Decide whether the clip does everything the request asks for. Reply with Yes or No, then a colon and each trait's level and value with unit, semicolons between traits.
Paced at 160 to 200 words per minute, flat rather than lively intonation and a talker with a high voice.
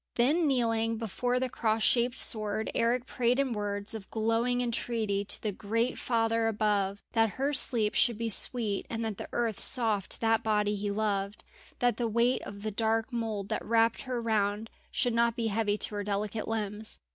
Yes: average, 185 wpm; narrow, 2.1 semitones; high, 225 Hz